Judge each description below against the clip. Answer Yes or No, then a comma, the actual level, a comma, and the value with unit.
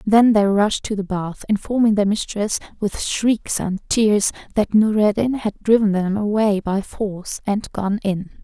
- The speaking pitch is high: Yes, high, 205 Hz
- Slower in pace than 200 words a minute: Yes, average, 170 wpm